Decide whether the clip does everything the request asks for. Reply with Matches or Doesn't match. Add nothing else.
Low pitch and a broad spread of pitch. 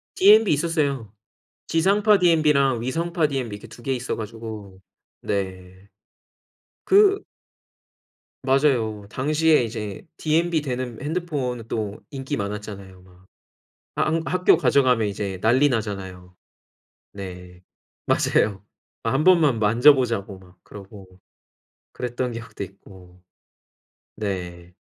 Matches